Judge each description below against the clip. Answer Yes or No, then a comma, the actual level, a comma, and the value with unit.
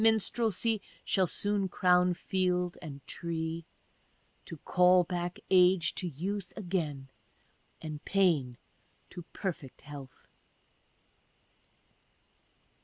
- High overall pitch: No, medium, 180 Hz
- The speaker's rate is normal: No, slow, 90 wpm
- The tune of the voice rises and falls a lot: No, average, 2.9 semitones